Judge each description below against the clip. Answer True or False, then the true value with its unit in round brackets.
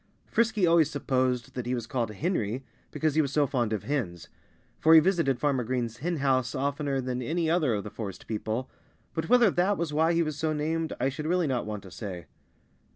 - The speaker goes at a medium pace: False (215 wpm)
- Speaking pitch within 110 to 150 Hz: True (140 Hz)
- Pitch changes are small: False (5.0 semitones)